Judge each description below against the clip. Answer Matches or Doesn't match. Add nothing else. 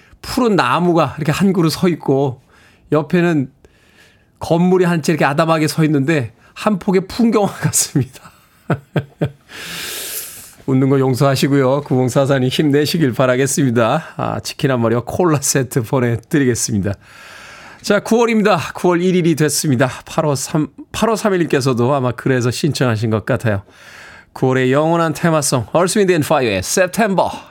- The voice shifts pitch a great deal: Doesn't match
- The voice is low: Doesn't match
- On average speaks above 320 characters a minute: Doesn't match